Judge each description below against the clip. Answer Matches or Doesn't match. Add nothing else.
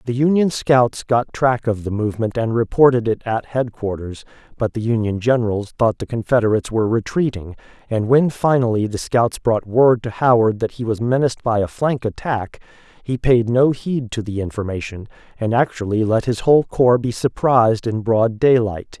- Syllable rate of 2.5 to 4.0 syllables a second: Doesn't match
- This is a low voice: Matches